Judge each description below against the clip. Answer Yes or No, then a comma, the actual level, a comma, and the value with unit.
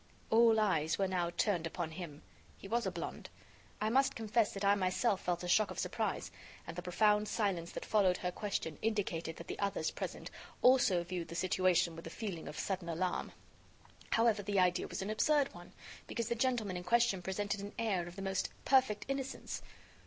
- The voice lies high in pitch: Yes, high, 195 Hz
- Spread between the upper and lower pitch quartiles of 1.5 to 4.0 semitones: Yes, average, 3.7 semitones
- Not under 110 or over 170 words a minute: No, average, 195 wpm